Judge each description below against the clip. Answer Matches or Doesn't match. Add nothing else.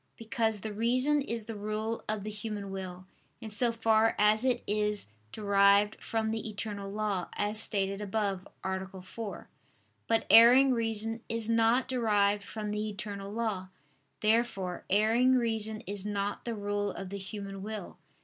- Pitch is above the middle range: Matches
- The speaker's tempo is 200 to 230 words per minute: Doesn't match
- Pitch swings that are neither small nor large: Doesn't match